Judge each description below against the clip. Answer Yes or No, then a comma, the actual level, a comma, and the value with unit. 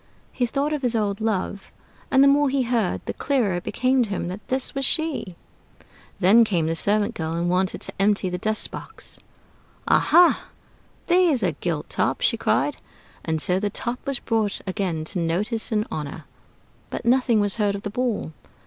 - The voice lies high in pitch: Yes, high, 210 Hz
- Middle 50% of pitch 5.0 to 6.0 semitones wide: Yes, wide, 5.4 semitones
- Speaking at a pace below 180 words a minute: No, average, 185 wpm